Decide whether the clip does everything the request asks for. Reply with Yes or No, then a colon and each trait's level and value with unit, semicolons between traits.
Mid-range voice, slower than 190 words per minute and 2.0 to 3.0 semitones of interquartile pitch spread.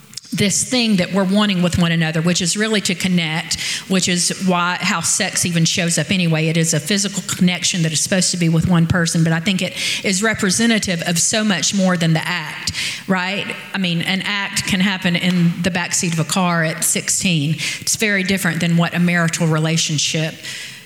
No: medium, 180 Hz; fast, 205 wpm; average, 2.7 semitones